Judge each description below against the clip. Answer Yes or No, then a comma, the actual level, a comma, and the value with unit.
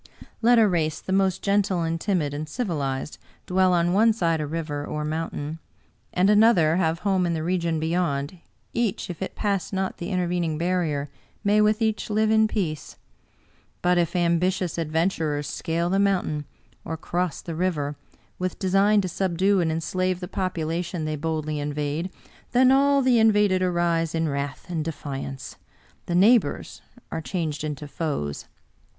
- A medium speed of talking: Yes, average, 165 wpm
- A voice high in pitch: No, medium, 175 Hz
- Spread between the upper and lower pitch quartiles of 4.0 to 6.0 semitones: No, average, 3.6 semitones